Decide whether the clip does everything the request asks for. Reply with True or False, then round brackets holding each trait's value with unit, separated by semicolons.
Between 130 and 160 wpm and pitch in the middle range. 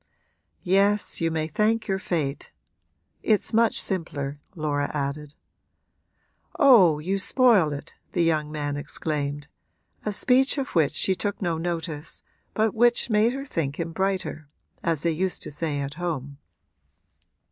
True (140 wpm; 165 Hz)